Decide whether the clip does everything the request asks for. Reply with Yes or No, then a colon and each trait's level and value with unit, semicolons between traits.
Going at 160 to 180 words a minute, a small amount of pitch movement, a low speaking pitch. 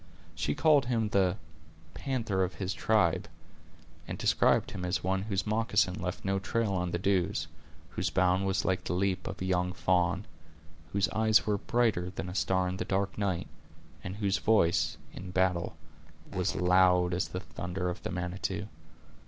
Yes: average, 170 wpm; narrow, 1.9 semitones; very low, 95 Hz